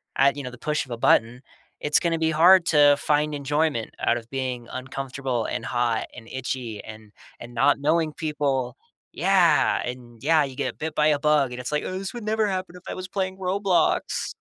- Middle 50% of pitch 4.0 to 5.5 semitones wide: Yes, average, 4.7 semitones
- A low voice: No, medium, 145 Hz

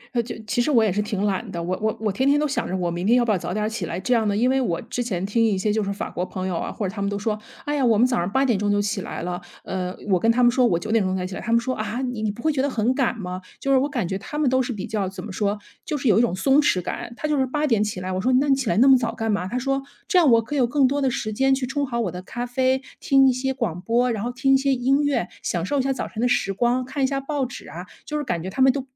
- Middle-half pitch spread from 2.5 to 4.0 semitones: No, average, 4.8 semitones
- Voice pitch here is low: No, high, 235 Hz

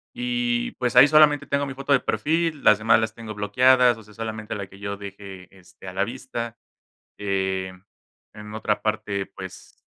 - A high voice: No, low, 110 Hz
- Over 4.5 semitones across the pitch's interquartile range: Yes, average, 5.1 semitones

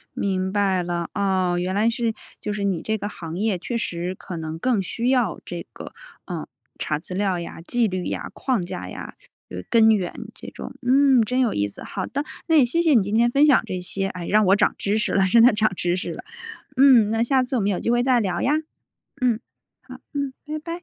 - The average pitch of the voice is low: No, high, 210 Hz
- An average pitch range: Yes, average, 5.0 semitones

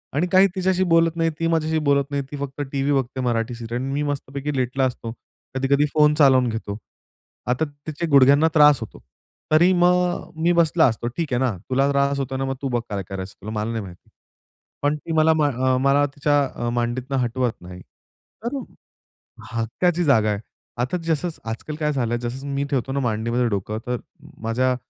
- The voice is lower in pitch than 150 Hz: Yes, low, 135 Hz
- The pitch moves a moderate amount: Yes, average, 3.9 semitones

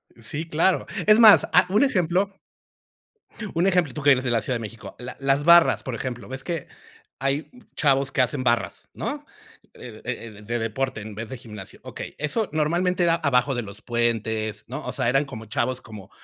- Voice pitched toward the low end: Yes, low, 130 Hz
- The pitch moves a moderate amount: No, wide, 5.9 semitones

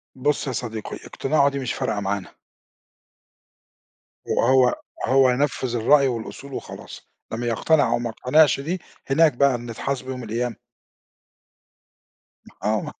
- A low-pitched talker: Yes, low, 130 Hz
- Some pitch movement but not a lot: Yes, average, 3.0 semitones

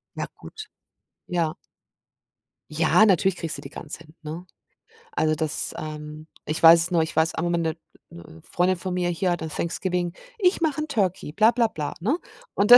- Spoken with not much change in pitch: No, average, 3.4 semitones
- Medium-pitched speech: Yes, medium, 170 Hz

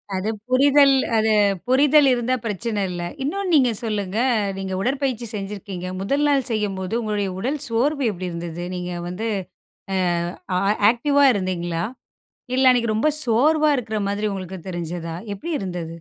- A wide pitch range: Yes, wide, 5.9 semitones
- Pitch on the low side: No, high, 215 Hz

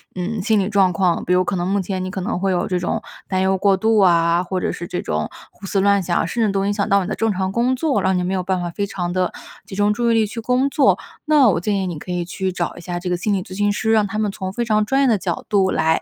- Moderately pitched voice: No, high, 195 Hz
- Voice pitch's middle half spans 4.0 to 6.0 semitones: No, average, 2.9 semitones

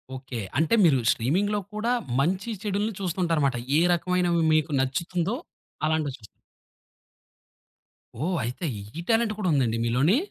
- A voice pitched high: No, medium, 170 Hz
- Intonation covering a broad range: Yes, wide, 6.1 semitones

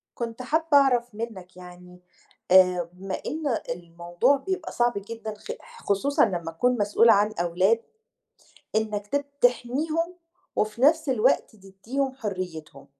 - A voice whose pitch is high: Yes, high, 215 Hz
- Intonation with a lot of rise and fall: Yes, wide, 5.7 semitones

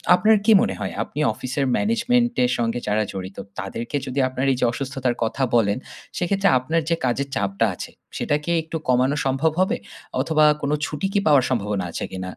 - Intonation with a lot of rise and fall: Yes, wide, 6.0 semitones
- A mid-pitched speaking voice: No, low, 130 Hz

